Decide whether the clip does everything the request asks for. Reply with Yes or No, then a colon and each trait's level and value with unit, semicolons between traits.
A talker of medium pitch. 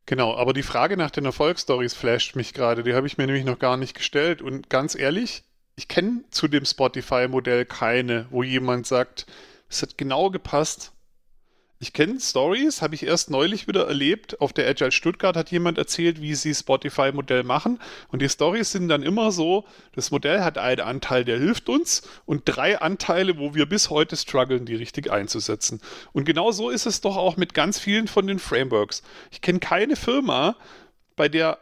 Yes: medium, 150 Hz